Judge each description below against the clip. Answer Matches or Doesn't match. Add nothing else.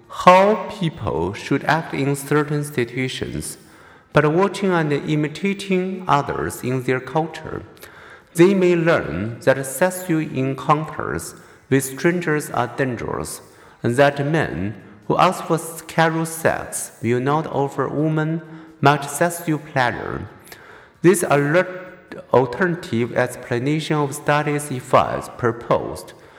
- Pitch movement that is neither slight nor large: Matches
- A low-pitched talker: Doesn't match